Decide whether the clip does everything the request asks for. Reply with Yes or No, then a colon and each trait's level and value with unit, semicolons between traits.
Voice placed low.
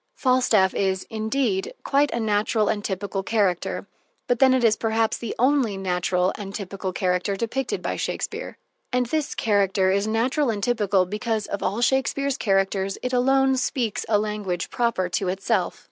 No: high, 210 Hz